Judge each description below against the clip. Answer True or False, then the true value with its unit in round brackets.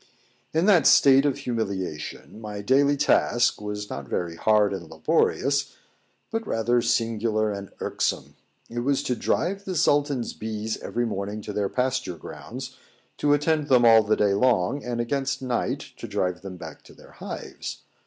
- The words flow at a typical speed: True (165 wpm)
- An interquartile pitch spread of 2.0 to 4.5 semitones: False (5.0 semitones)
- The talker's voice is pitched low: True (120 Hz)